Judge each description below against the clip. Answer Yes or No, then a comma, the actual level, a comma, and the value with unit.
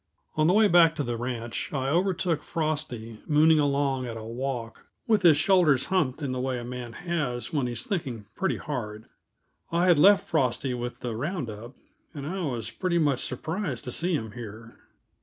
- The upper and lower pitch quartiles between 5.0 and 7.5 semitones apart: Yes, wide, 5.4 semitones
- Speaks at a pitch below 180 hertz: Yes, medium, 140 Hz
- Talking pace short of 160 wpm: No, average, 190 wpm